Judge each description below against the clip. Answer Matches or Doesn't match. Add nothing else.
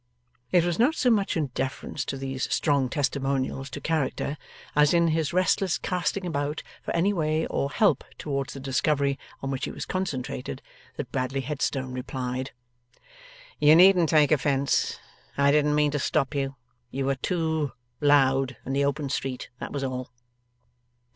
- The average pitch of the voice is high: Doesn't match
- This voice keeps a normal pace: Matches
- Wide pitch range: Doesn't match